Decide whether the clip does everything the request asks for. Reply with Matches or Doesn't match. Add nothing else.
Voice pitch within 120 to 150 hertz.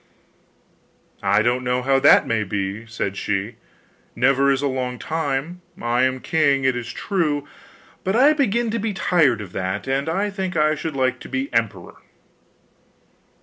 Matches